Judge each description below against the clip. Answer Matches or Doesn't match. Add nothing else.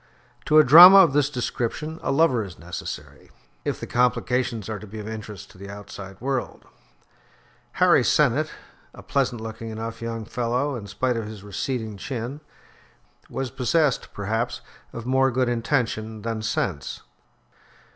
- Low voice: Matches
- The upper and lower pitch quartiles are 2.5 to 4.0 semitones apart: Matches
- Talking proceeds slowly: Doesn't match